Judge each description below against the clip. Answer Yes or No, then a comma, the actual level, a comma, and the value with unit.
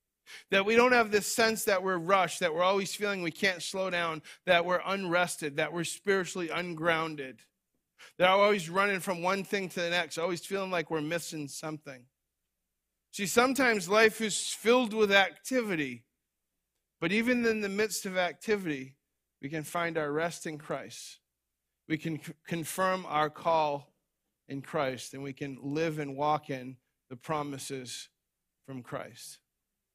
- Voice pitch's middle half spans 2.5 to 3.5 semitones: No, average, 5.1 semitones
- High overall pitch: No, medium, 170 Hz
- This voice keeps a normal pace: Yes, average, 160 wpm